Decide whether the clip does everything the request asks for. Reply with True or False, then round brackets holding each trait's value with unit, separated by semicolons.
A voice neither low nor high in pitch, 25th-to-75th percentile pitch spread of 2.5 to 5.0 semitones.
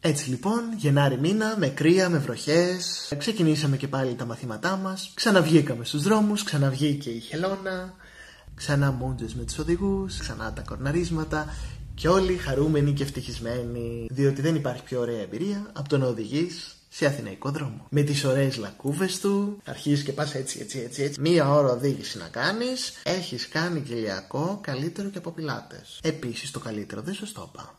False (145 Hz; 5.6 semitones)